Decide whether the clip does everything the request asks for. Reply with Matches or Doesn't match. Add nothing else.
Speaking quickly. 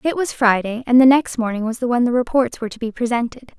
Matches